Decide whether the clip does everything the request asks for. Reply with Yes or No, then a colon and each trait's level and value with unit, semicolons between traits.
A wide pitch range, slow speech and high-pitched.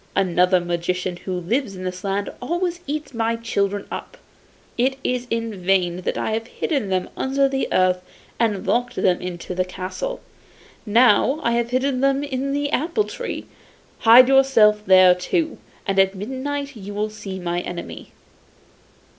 No: wide, 6.4 semitones; average, 160 wpm; high, 220 Hz